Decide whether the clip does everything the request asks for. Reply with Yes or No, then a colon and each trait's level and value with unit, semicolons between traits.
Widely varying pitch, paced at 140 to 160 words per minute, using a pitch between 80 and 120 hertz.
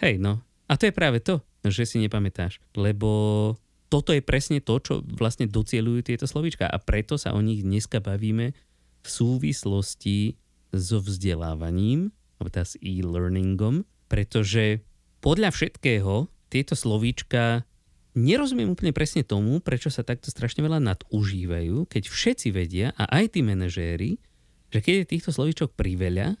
Yes: wide, 6.3 semitones; average, 145 wpm; low, 110 Hz